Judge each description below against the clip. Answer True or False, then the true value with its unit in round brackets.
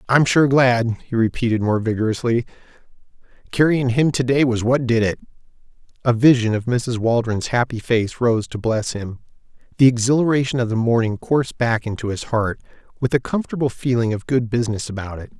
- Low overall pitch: True (120 Hz)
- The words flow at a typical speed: True (175 wpm)